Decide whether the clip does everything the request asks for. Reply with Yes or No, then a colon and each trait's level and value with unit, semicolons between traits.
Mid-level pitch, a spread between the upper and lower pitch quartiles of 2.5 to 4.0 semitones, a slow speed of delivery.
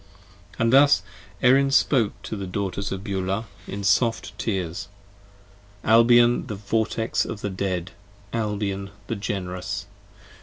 No: low, 105 Hz; average, 3.0 semitones; slow, 120 wpm